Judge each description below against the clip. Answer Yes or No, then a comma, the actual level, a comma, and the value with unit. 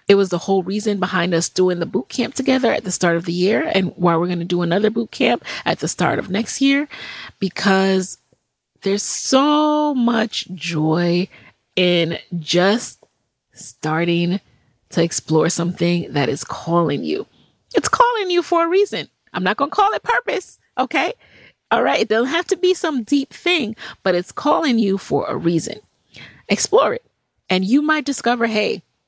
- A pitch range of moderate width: No, wide, 7.5 semitones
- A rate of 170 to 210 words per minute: Yes, average, 180 wpm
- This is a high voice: Yes, high, 195 Hz